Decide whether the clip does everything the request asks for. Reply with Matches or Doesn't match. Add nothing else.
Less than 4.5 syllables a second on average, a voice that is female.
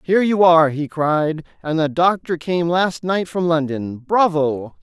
Doesn't match